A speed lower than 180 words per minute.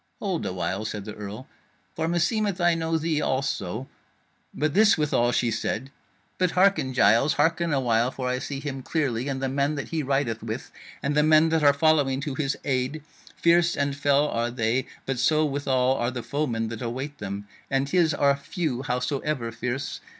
No: average, 190 wpm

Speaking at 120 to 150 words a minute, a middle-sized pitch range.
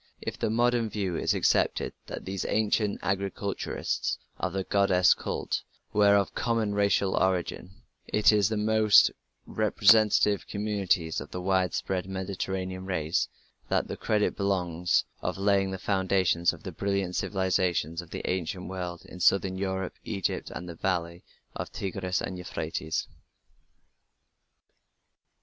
No: average, 140 wpm; narrow, 2.1 semitones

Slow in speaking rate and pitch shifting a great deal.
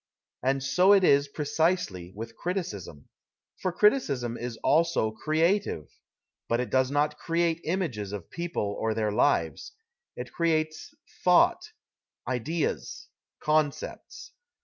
Yes: slow, 125 wpm; wide, 6.6 semitones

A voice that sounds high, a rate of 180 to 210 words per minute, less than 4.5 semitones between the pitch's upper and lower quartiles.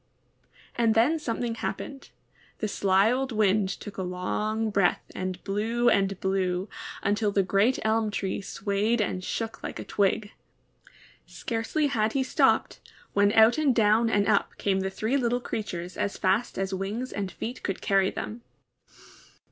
No: high, 210 Hz; average, 155 wpm; average, 2.9 semitones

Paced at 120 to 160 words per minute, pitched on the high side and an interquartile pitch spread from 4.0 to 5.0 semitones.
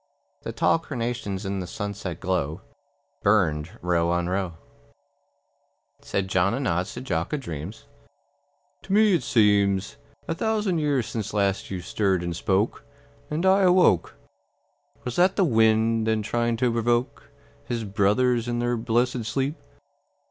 No: average, 145 wpm; low, 110 Hz; average, 4.7 semitones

